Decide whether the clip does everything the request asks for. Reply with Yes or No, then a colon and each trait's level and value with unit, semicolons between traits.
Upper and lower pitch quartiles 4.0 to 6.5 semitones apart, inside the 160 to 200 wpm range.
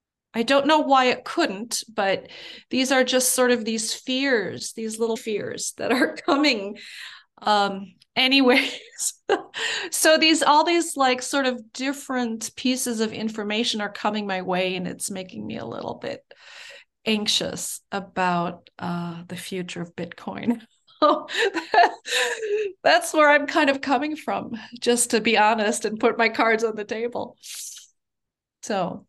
No: average, 4.9 semitones; average, 145 wpm